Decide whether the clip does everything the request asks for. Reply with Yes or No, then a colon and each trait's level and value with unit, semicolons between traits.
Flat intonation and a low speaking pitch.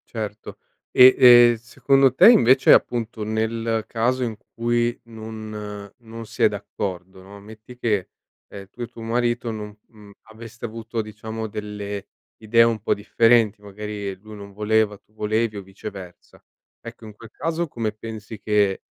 Yes: narrow, 1.9 semitones; low, 110 Hz